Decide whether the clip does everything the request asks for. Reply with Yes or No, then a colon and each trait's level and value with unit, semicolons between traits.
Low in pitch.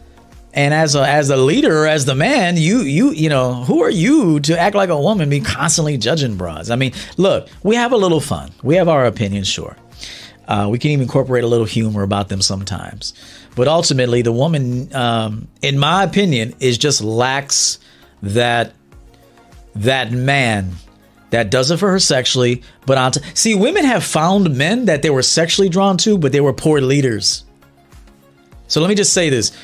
Yes: low, 130 Hz